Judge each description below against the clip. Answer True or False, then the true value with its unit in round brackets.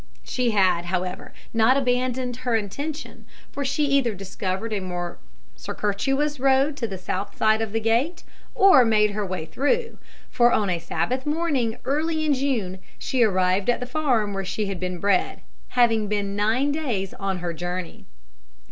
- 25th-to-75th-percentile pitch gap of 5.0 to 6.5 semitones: True (5.6 semitones)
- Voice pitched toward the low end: False (225 Hz)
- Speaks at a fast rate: False (165 wpm)